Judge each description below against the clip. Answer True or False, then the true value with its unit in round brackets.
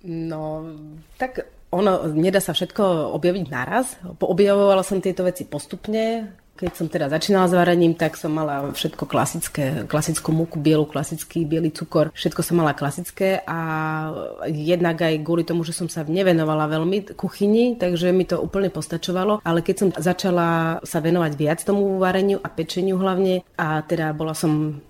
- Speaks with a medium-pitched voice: True (170 Hz)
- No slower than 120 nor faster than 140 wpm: False (160 wpm)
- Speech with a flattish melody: False (3.1 semitones)